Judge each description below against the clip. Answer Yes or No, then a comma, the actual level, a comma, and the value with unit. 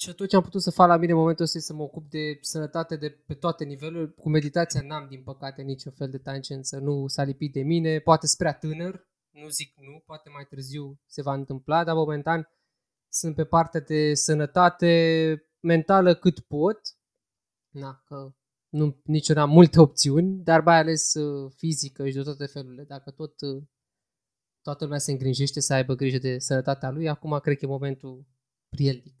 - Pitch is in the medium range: Yes, medium, 150 Hz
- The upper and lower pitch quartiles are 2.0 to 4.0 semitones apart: Yes, average, 2.7 semitones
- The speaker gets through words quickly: Yes, fast, 185 wpm